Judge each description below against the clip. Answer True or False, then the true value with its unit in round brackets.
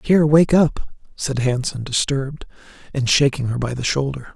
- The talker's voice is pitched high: False (135 Hz)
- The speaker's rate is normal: True (165 wpm)